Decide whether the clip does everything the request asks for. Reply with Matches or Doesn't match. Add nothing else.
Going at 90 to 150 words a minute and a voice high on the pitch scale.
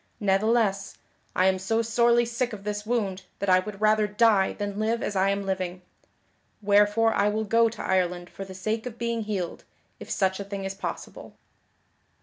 Doesn't match